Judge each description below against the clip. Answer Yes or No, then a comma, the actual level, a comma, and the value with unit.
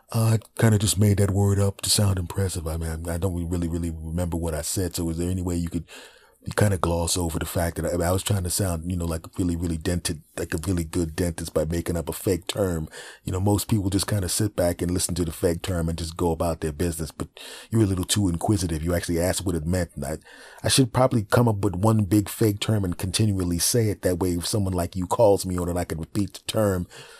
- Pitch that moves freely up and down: No, average, 3.0 semitones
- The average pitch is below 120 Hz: Yes, very low, 90 Hz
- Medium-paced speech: No, fast, 270 wpm